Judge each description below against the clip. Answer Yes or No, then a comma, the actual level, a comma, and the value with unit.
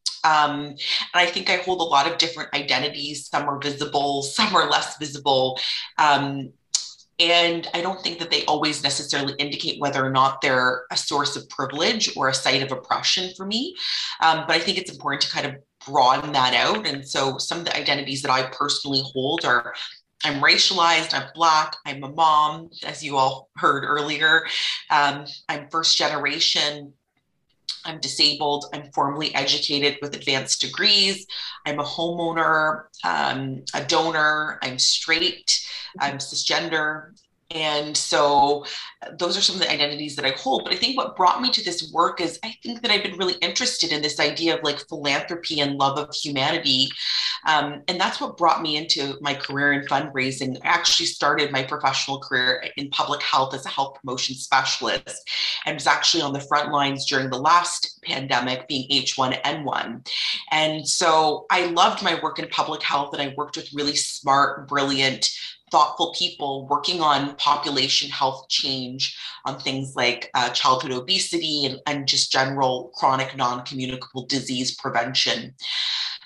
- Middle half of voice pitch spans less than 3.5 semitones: Yes, average, 2.9 semitones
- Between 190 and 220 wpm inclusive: No, average, 170 wpm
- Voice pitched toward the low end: No, medium, 145 Hz